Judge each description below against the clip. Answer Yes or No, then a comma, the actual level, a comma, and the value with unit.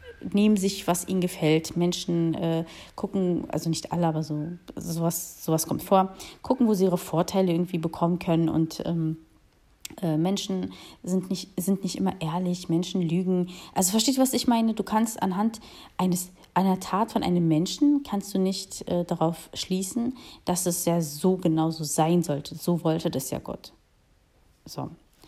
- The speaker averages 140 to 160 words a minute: No, average, 170 wpm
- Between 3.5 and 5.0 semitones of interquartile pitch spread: No, average, 2.7 semitones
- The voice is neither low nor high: Yes, medium, 180 Hz